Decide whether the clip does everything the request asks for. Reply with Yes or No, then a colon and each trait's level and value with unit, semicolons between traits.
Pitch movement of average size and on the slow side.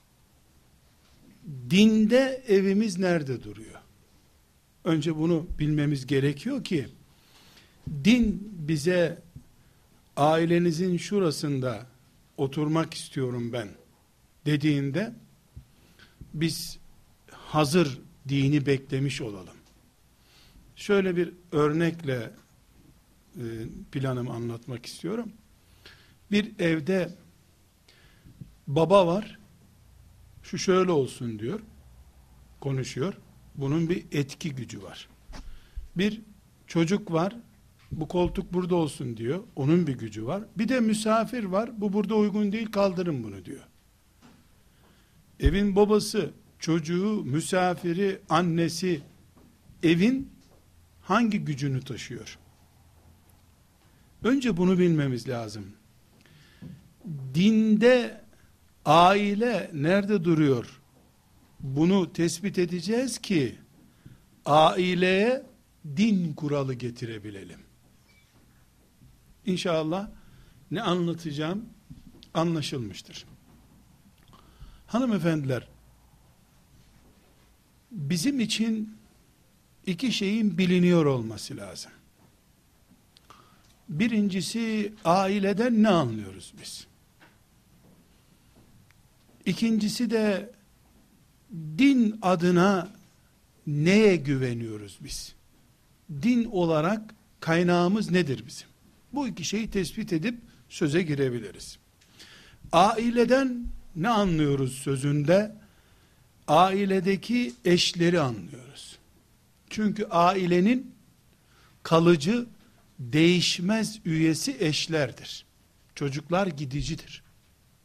No: wide, 6.7 semitones; slow, 70 wpm